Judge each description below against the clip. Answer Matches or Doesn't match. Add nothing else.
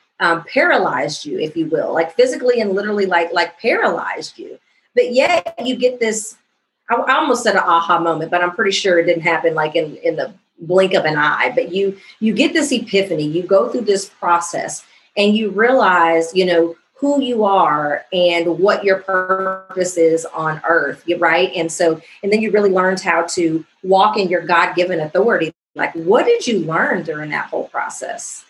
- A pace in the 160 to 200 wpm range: Matches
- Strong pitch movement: Doesn't match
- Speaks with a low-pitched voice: Doesn't match